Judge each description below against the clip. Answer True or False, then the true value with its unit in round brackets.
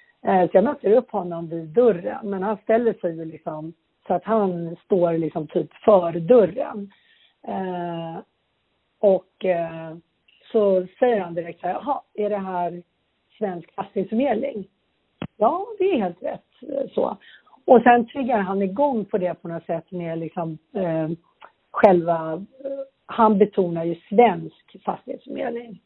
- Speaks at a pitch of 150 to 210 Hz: True (190 Hz)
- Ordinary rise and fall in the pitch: True (4.9 semitones)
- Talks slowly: False (140 wpm)